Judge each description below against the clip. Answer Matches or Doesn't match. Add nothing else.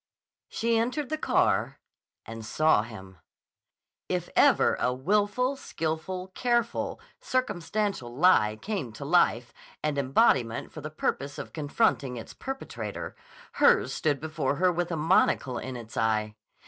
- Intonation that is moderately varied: Doesn't match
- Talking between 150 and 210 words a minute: Doesn't match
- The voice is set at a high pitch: Doesn't match